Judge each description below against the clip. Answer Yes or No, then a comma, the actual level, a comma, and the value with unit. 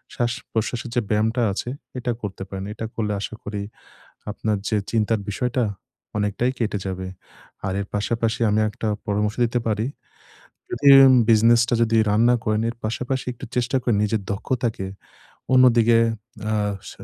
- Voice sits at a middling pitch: No, low, 110 Hz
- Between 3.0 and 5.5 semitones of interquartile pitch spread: No, narrow, 2.4 semitones